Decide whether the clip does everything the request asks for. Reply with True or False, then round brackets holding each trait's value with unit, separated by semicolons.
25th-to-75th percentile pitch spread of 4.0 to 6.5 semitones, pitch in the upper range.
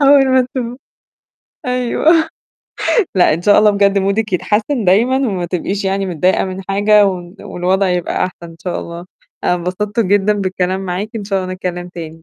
False (2.7 semitones; 195 Hz)